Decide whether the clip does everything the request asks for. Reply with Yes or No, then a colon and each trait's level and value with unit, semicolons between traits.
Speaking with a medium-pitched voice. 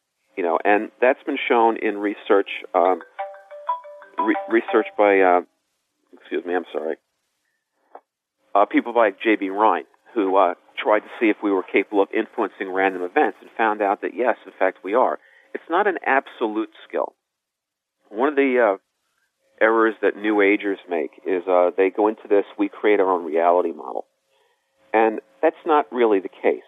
No: low, 110 Hz